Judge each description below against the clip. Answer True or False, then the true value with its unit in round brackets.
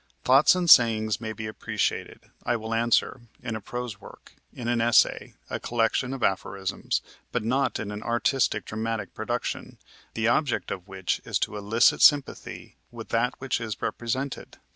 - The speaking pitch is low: True (115 Hz)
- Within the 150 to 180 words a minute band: True (165 wpm)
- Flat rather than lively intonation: True (2.2 semitones)